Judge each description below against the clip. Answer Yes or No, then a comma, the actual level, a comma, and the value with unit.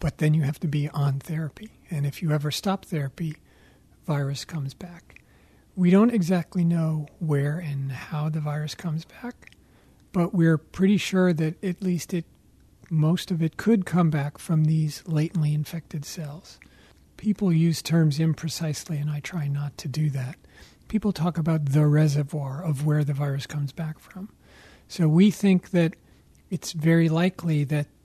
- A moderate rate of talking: Yes, average, 165 wpm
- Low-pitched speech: No, medium, 160 Hz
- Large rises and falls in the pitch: No, average, 2.8 semitones